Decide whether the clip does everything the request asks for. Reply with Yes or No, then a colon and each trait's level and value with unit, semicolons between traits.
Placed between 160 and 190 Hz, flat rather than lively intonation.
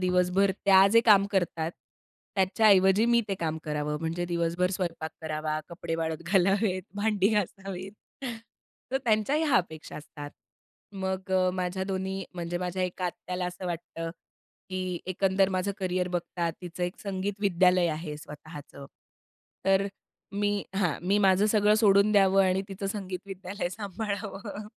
Yes: medium, 185 Hz; narrow, 2.2 semitones